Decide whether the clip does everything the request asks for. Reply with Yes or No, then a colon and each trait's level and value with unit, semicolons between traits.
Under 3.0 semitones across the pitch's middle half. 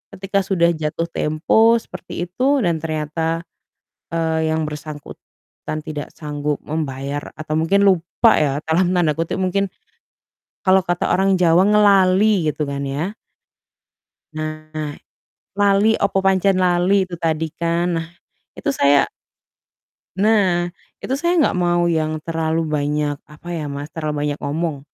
No: average, 3.5 semitones